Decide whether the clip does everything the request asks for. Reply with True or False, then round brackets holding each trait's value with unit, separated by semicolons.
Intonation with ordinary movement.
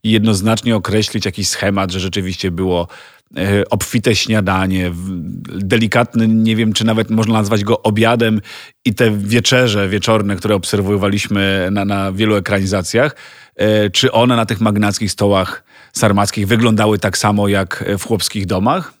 False (2.0 semitones)